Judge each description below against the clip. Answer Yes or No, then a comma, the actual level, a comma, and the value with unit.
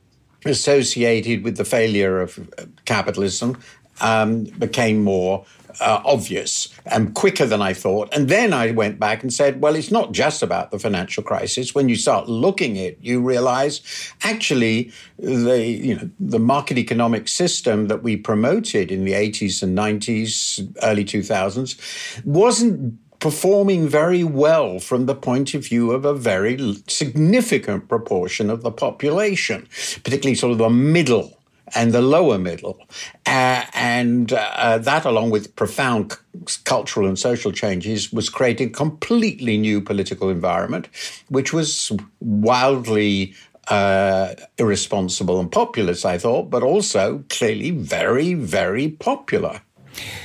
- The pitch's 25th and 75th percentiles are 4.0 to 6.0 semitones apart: Yes, average, 4.9 semitones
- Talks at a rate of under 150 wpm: Yes, average, 140 wpm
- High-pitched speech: No, low, 120 Hz